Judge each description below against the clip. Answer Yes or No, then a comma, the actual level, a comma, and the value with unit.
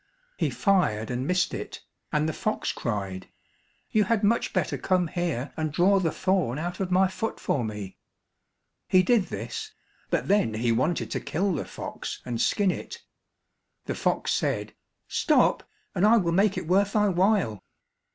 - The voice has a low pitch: No, medium, 180 Hz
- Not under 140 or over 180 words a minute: Yes, average, 170 wpm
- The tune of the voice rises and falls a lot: Yes, wide, 7.5 semitones